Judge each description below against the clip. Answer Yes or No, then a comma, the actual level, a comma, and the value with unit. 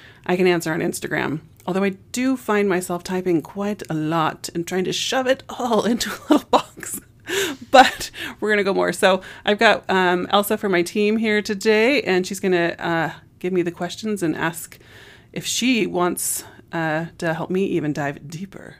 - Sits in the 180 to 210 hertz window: Yes, medium, 185 Hz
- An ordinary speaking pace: Yes, average, 195 wpm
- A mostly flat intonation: No, average, 4.0 semitones